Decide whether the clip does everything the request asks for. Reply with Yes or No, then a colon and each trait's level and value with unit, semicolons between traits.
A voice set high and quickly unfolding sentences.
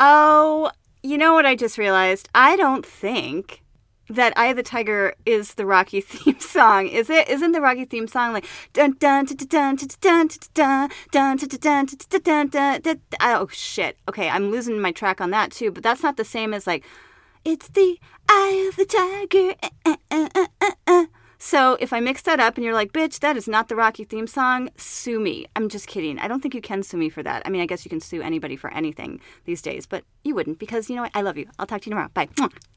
Yes: very high, 260 Hz; fast, 220 wpm